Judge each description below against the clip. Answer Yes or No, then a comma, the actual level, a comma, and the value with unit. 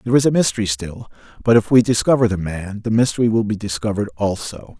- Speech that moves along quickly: Yes, fast, 215 wpm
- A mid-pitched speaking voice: No, low, 110 Hz